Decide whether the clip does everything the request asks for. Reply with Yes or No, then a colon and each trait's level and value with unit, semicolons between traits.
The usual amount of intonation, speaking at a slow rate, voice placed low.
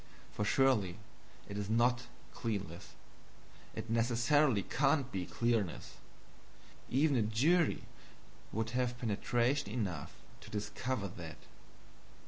Yes: average, 4.0 semitones; slow, 105 wpm; low, 115 Hz